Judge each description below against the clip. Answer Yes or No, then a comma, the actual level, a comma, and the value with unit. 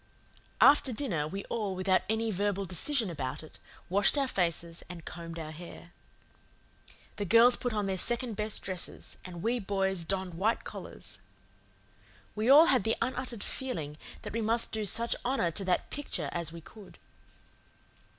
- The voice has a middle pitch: No, high, 200 Hz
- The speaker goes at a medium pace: Yes, average, 160 wpm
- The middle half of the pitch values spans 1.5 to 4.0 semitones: No, average, 5.0 semitones